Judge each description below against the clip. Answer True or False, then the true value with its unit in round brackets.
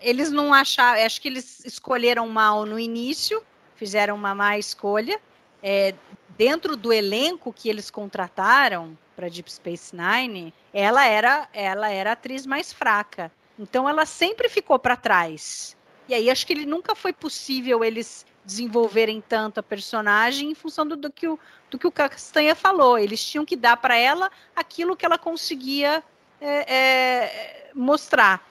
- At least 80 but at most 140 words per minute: False (160 wpm)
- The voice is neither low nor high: False (245 Hz)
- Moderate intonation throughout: False (6.2 semitones)